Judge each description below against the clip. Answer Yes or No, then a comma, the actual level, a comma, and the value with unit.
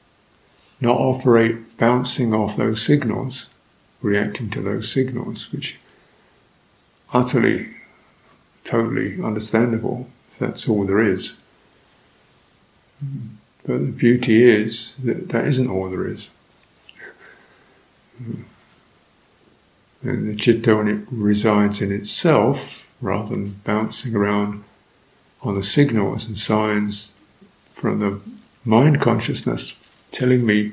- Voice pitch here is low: Yes, low, 110 Hz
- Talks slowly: Yes, slow, 100 wpm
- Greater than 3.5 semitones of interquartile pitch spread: No, average, 2.8 semitones